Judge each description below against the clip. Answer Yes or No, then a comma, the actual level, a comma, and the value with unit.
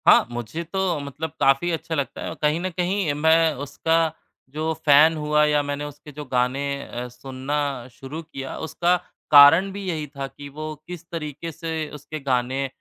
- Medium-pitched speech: Yes, medium, 150 Hz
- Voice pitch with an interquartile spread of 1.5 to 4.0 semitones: Yes, average, 2.9 semitones